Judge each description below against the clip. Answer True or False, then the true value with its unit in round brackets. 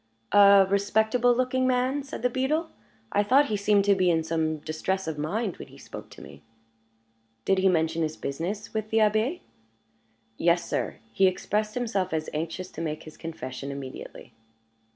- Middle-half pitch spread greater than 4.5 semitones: True (5.4 semitones)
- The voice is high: True (195 Hz)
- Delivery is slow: False (175 wpm)